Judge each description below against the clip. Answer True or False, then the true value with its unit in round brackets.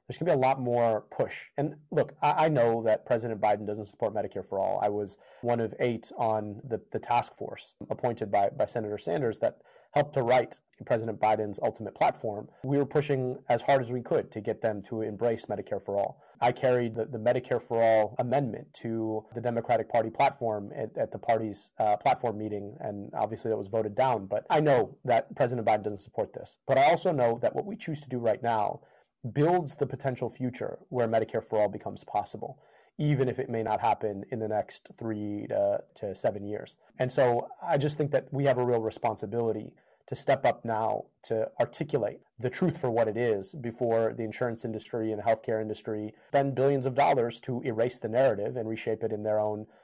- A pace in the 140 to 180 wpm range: False (205 wpm)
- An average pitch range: True (3.1 semitones)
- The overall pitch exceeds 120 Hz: False (115 Hz)